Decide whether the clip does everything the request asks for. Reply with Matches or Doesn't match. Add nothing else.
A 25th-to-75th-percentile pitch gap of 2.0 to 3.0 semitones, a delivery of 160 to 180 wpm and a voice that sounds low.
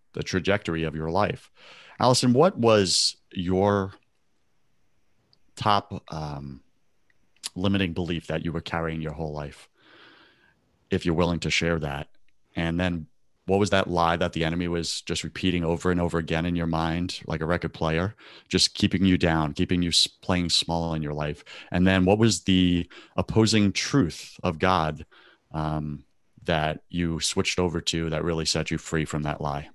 Matches